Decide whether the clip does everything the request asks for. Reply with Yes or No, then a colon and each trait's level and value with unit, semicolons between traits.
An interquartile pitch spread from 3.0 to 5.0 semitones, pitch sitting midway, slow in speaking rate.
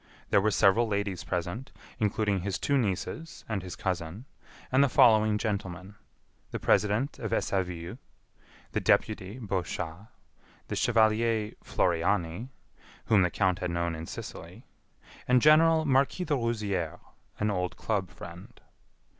No: average, 4.3 semitones; low, 105 Hz; slow, 130 wpm